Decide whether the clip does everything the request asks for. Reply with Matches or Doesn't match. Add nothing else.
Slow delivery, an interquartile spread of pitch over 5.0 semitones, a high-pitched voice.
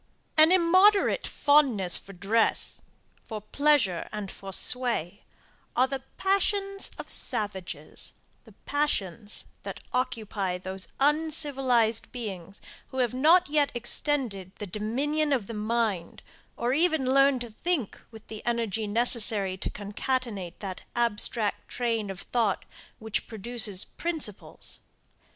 Matches